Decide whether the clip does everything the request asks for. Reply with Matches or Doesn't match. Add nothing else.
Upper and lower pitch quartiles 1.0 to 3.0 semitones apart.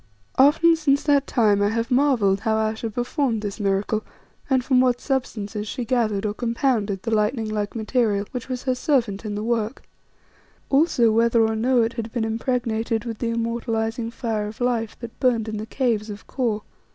Matches